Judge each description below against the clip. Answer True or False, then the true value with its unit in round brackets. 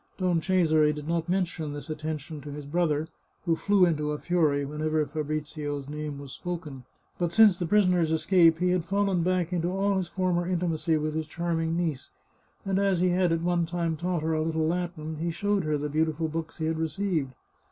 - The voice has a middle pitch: True (165 Hz)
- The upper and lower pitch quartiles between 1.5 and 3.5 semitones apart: True (2.6 semitones)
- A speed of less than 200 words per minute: False (205 wpm)